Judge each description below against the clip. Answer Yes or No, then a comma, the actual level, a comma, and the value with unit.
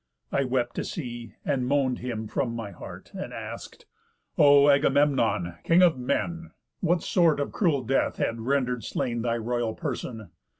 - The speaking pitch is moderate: No, low, 125 Hz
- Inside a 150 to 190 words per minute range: Yes, average, 160 wpm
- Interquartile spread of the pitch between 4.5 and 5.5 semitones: No, average, 3.5 semitones